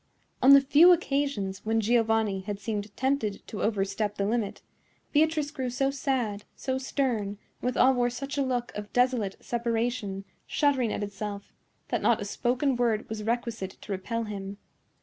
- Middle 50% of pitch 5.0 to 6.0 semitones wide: No, average, 4.2 semitones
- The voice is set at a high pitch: Yes, high, 230 Hz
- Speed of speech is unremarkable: Yes, average, 165 wpm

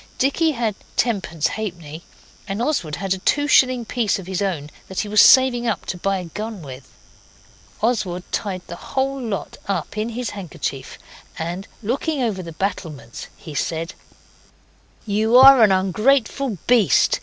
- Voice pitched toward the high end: Yes, high, 205 Hz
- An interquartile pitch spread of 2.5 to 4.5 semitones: No, wide, 5.4 semitones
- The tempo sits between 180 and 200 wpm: No, average, 155 wpm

